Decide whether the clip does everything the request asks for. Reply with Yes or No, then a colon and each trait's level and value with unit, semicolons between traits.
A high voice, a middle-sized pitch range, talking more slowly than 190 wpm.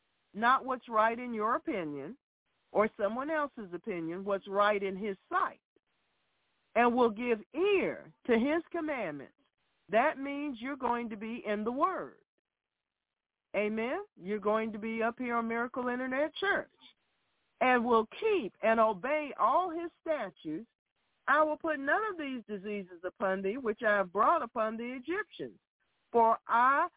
No: high, 235 Hz; wide, 6.1 semitones; average, 150 wpm